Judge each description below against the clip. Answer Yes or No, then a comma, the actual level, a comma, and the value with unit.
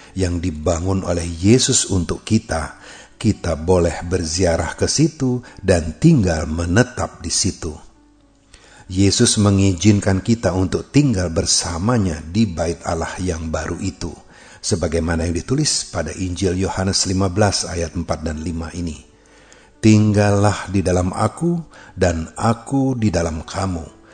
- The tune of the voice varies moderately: Yes, average, 4.0 semitones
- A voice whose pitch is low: Yes, very low, 95 Hz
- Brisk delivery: No, average, 120 wpm